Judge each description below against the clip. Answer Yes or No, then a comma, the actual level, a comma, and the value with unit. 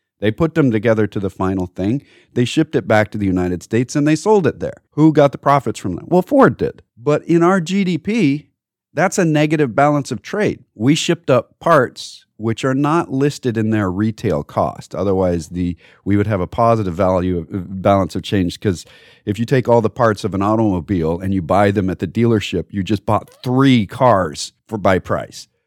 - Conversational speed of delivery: No, fast, 210 wpm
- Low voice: Yes, low, 110 Hz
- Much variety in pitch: Yes, wide, 6.7 semitones